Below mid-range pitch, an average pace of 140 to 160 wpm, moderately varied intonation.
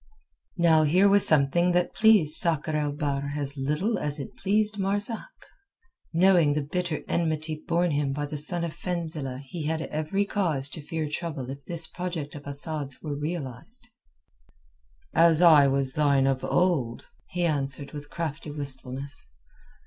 No: medium, 155 Hz; average, 155 wpm; average, 3.4 semitones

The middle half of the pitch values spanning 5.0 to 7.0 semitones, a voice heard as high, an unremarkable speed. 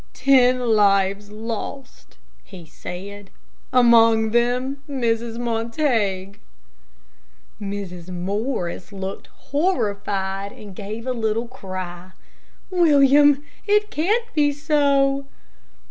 No: wide, 5.6 semitones; high, 230 Hz; slow, 85 wpm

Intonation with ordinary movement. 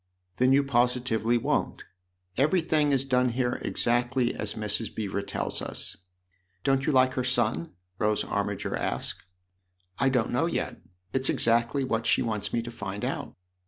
Yes: average, 3.3 semitones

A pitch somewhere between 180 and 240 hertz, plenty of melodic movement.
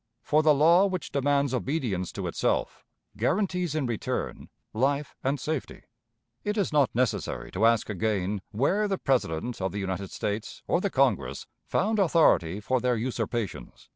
No: low, 130 Hz; wide, 6.8 semitones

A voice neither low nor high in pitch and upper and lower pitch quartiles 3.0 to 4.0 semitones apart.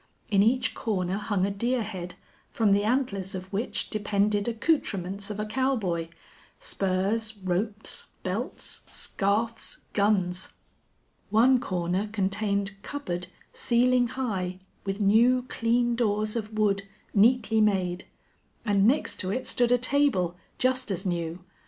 No: high, 210 Hz; average, 3.5 semitones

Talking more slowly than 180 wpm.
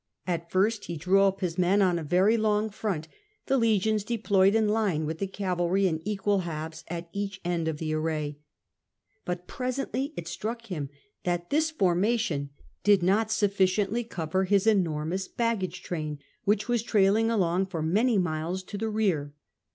Yes: average, 165 wpm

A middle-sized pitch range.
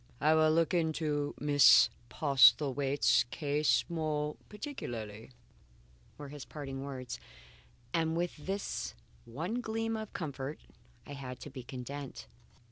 Yes: average, 3.3 semitones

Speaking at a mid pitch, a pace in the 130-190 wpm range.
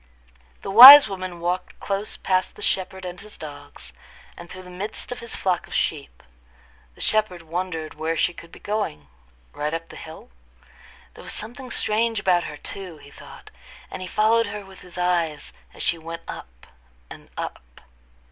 Yes: medium, 180 Hz; average, 175 wpm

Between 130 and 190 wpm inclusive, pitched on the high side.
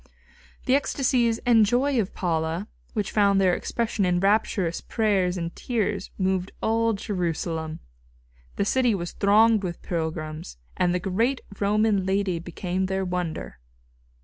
Yes: slow, 135 wpm; high, 195 Hz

